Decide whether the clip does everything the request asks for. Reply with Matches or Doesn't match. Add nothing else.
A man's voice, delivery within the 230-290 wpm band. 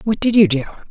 Doesn't match